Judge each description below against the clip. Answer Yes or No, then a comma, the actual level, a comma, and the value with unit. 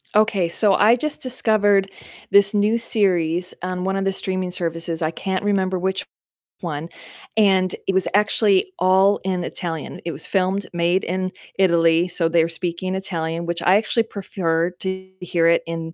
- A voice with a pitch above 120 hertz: Yes, medium, 185 Hz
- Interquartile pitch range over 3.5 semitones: No, narrow, 2.6 semitones